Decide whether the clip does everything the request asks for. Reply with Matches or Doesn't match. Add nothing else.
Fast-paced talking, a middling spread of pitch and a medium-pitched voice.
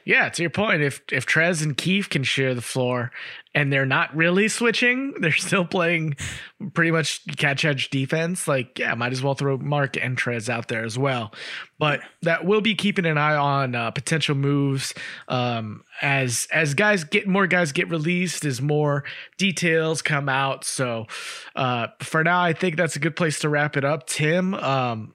Doesn't match